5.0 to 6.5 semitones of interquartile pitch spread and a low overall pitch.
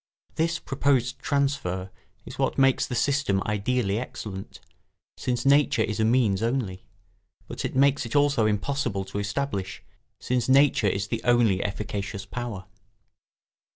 Yes: average, 5.3 semitones; low, 115 Hz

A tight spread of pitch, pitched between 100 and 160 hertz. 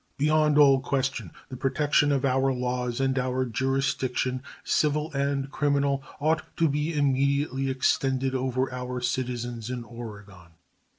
Yes: narrow, 2.0 semitones; low, 135 Hz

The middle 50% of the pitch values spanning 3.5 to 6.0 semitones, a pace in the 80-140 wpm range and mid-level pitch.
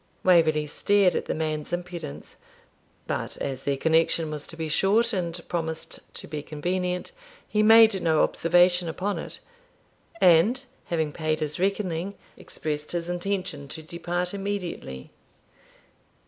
No: average, 3.1 semitones; slow, 135 wpm; medium, 170 Hz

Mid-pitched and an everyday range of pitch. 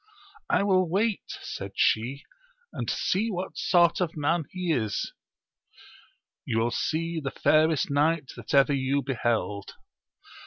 Yes: medium, 155 Hz; average, 4.5 semitones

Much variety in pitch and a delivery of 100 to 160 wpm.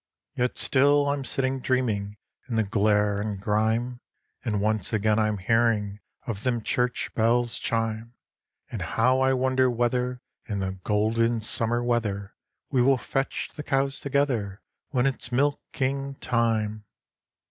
No: average, 3.3 semitones; slow, 135 wpm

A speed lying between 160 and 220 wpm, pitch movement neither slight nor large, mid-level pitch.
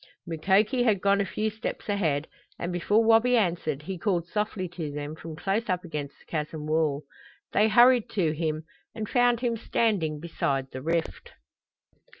No: average, 165 wpm; wide, 5.7 semitones; medium, 180 Hz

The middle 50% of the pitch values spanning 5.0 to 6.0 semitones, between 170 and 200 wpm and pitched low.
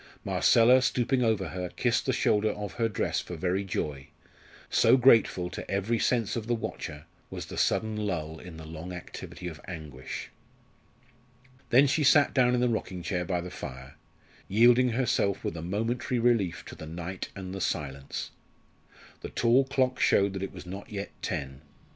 Yes: average, 5.3 semitones; average, 175 wpm; low, 100 Hz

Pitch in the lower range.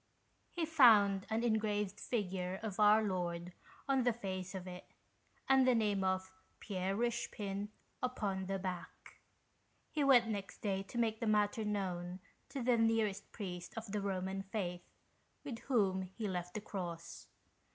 No: high, 200 Hz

